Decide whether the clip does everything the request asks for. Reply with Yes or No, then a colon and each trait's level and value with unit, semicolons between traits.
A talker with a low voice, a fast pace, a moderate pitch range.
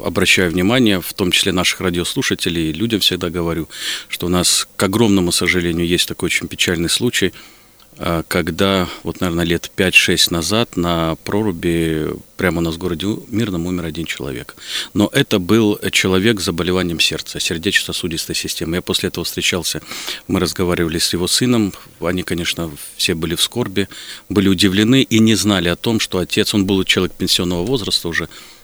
Yes: very low, 90 Hz; fast, 165 wpm; average, 3.2 semitones